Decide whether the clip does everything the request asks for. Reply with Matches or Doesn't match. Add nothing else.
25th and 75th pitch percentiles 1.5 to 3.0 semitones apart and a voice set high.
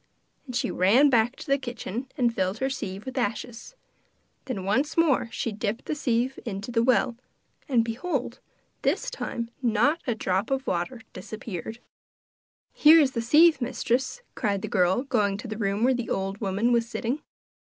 Doesn't match